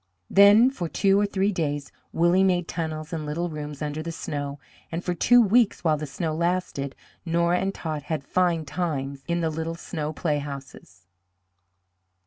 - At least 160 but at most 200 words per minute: Yes, average, 165 wpm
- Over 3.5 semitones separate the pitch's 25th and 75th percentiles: No, average, 3.2 semitones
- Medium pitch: Yes, medium, 165 Hz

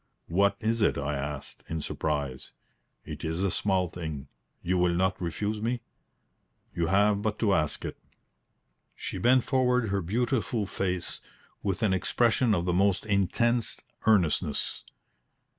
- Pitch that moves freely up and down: No, average, 4.3 semitones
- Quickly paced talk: No, average, 140 wpm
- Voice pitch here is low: Yes, very low, 95 Hz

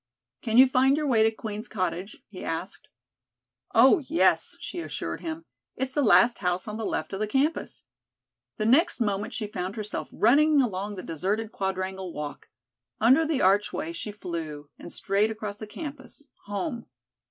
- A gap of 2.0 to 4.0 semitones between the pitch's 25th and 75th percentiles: No, wide, 5.5 semitones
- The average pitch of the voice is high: Yes, high, 215 Hz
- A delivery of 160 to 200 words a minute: Yes, average, 165 wpm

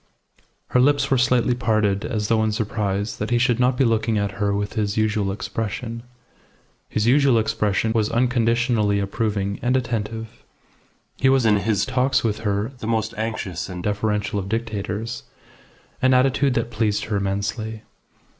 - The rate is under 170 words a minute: Yes, average, 160 wpm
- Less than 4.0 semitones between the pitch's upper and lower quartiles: Yes, narrow, 2.5 semitones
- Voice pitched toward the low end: Yes, low, 110 Hz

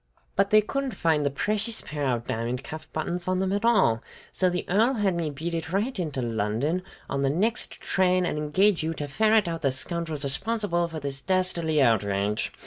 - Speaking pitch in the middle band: Yes, medium, 165 Hz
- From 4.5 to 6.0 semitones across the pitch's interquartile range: Yes, wide, 5.6 semitones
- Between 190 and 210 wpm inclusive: Yes, average, 200 wpm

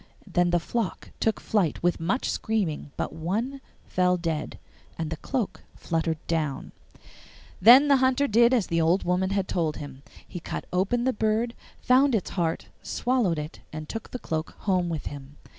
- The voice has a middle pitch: Yes, medium, 180 Hz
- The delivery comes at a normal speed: Yes, average, 175 wpm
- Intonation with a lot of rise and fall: Yes, wide, 6.2 semitones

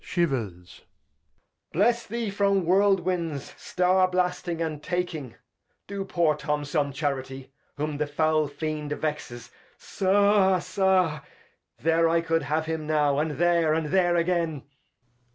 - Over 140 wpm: No, slow, 135 wpm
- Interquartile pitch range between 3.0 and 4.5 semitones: Yes, average, 3.6 semitones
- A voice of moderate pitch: Yes, medium, 165 Hz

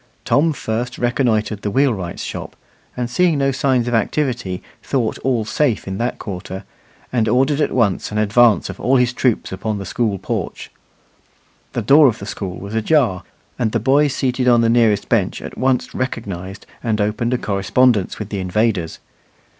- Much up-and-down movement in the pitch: No, average, 3.9 semitones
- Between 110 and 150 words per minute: No, average, 170 wpm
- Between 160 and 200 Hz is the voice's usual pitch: No, low, 115 Hz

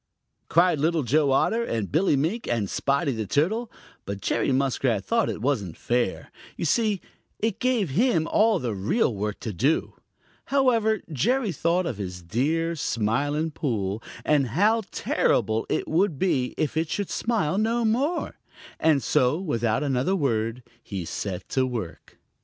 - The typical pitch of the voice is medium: Yes, medium, 145 Hz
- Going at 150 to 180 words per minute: Yes, average, 160 wpm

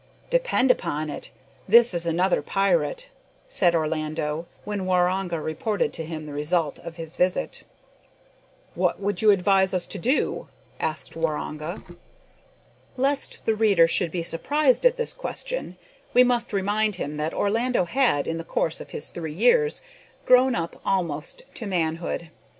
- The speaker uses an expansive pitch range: Yes, wide, 6.1 semitones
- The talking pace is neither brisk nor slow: Yes, average, 150 wpm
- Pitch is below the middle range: No, medium, 185 Hz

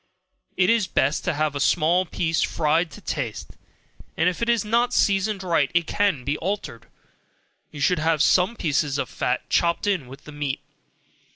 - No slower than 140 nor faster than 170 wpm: No, average, 180 wpm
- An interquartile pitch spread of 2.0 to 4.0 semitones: No, average, 4.8 semitones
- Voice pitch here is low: No, medium, 165 Hz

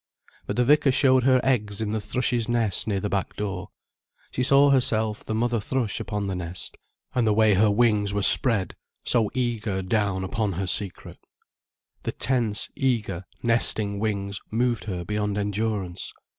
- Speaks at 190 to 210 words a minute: No, average, 165 wpm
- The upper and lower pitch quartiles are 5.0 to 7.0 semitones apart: No, average, 3.0 semitones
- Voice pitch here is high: No, low, 105 Hz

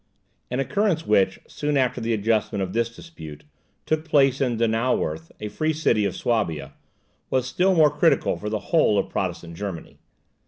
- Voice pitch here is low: Yes, low, 115 Hz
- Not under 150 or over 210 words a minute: Yes, average, 165 wpm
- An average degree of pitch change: No, wide, 6.5 semitones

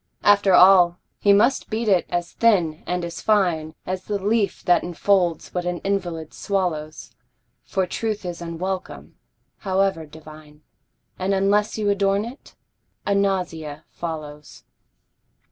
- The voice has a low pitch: No, medium, 185 Hz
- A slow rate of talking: Yes, slow, 130 wpm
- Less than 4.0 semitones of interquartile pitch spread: Yes, average, 3.2 semitones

